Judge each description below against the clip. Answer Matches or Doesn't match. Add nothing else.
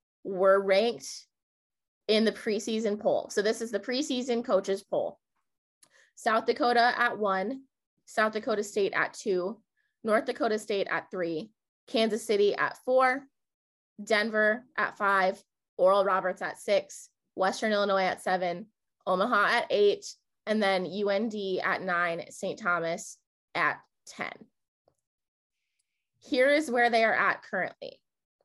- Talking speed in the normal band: Doesn't match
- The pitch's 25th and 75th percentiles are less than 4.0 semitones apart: Doesn't match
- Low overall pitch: Doesn't match